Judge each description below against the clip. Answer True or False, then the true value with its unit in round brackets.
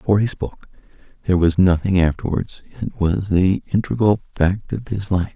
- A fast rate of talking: False (170 wpm)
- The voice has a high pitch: False (95 Hz)